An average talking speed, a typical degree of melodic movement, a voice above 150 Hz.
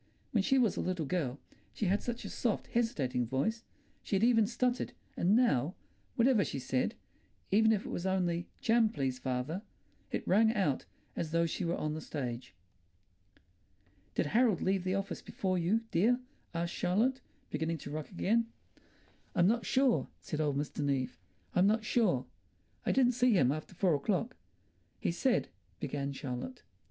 No: average, 165 wpm; wide, 7.2 semitones; medium, 185 Hz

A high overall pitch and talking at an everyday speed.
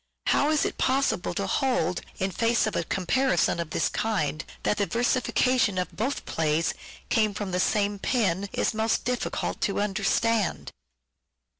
Yes: high, 210 Hz; average, 160 wpm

